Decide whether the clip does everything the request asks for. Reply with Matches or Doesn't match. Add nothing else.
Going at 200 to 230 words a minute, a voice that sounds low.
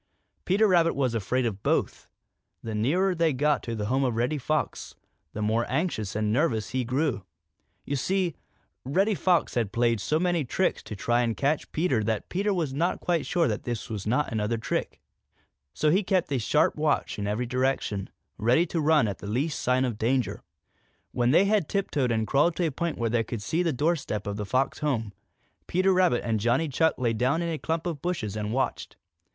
Matches